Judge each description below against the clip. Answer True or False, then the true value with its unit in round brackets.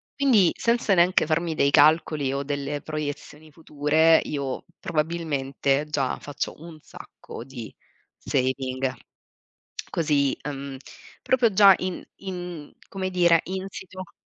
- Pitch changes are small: False (4.1 semitones)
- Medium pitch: True (155 Hz)